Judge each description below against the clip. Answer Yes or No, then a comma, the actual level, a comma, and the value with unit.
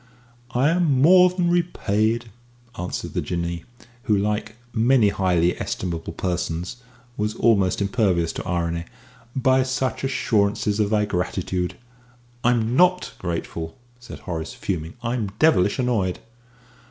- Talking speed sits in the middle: No, slow, 120 wpm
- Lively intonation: Yes, wide, 5.9 semitones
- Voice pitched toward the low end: Yes, low, 105 Hz